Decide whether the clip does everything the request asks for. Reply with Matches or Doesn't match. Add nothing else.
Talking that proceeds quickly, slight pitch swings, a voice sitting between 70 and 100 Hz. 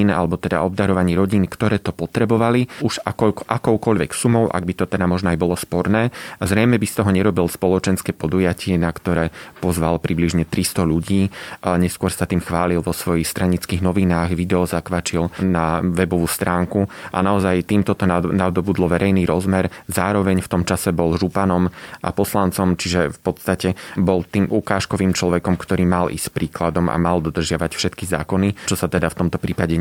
Matches